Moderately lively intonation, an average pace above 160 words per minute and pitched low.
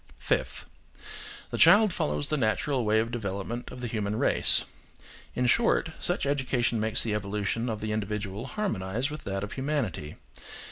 No: average, 4.4 semitones; average, 155 wpm; low, 110 Hz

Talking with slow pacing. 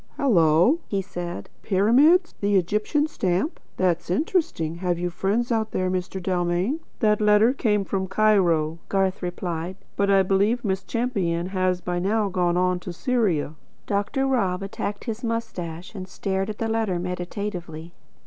No: average, 150 wpm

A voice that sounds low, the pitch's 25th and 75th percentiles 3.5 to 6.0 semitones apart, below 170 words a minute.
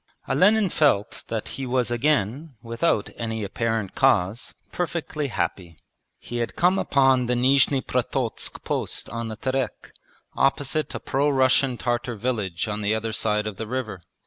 Yes: low, 120 Hz; average, 3.9 semitones; average, 150 wpm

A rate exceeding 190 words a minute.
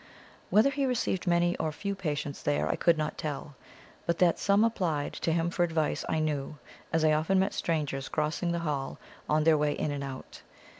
Yes: average, 200 wpm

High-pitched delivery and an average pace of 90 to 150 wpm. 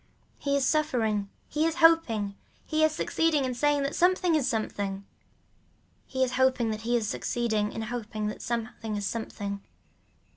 No: high, 240 Hz; average, 160 wpm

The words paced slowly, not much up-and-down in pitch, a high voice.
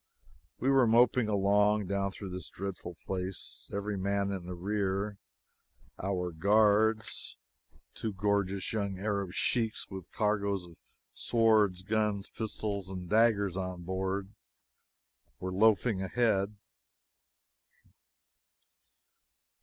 No: slow, 105 wpm; narrow, 2.1 semitones; low, 100 Hz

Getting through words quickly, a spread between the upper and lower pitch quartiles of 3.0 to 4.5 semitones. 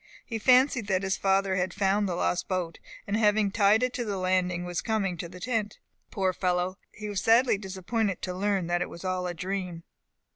No: fast, 210 wpm; narrow, 2.5 semitones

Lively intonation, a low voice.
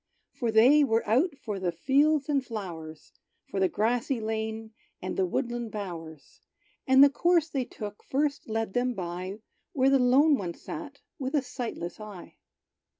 No: wide, 5.7 semitones; high, 230 Hz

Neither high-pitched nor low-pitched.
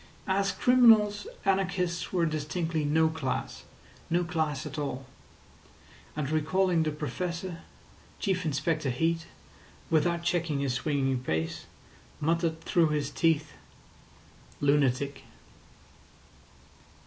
Yes: medium, 160 Hz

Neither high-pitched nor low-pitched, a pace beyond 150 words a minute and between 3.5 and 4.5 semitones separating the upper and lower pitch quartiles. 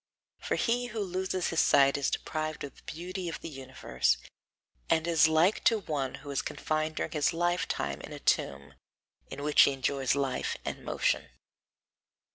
Yes: medium, 155 Hz; average, 170 wpm; average, 4.0 semitones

